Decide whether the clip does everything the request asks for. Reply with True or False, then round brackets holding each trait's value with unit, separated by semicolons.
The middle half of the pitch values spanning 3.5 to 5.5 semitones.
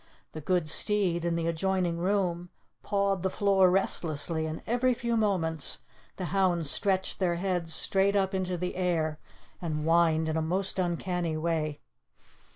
False (2.8 semitones)